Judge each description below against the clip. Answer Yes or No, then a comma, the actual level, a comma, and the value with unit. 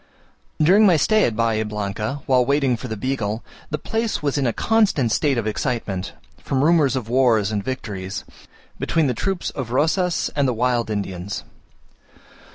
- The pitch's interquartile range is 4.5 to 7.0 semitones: Yes, average, 5.3 semitones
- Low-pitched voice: Yes, low, 125 Hz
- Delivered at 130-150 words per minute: No, average, 165 wpm